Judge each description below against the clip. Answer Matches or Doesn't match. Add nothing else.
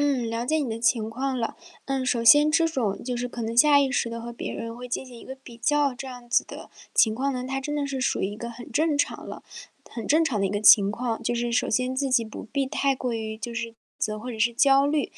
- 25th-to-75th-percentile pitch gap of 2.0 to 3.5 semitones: Matches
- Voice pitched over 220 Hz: Matches